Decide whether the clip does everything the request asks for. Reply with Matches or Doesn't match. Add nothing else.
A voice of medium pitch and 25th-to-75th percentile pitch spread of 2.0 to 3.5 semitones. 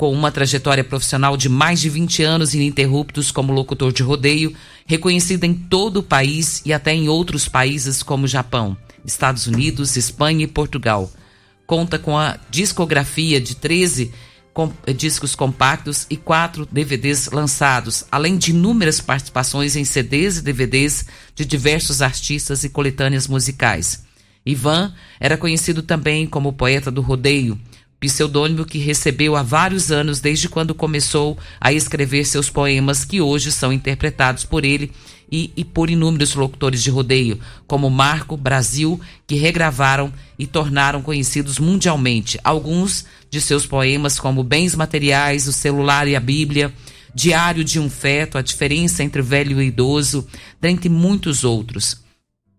Matches